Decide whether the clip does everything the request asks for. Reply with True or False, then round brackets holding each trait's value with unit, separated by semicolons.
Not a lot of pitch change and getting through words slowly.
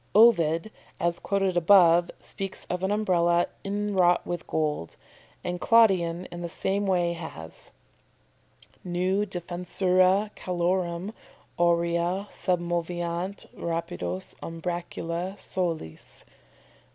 True (2.0 semitones; 90 wpm)